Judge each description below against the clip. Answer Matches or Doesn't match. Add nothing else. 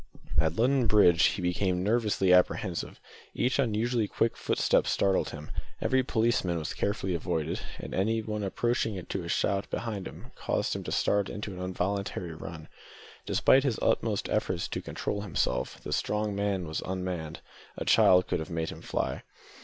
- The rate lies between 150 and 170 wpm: Matches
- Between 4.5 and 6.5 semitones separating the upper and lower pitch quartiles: Doesn't match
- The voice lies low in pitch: Matches